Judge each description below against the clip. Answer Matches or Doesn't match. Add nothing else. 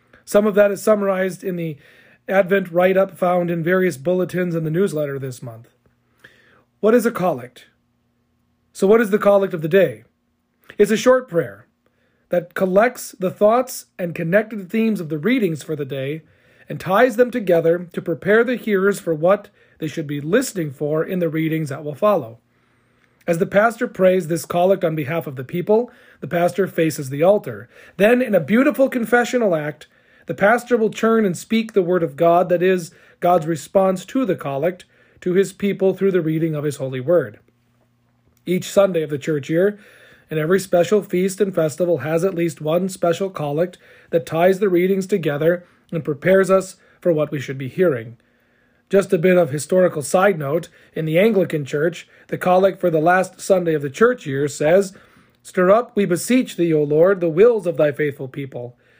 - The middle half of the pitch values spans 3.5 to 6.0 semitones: Matches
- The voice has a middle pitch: Matches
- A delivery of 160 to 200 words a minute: Matches